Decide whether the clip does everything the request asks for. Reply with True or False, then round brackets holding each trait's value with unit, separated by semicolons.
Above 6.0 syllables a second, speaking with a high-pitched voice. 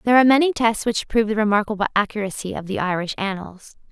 True (6.9 syllables/s; 215 Hz)